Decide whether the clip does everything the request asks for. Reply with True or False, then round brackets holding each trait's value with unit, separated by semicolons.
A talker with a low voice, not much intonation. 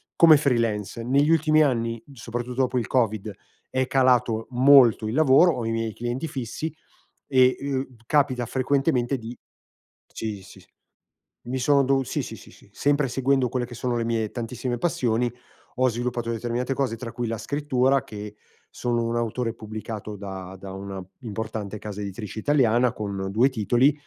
False (120 Hz; 3.0 semitones)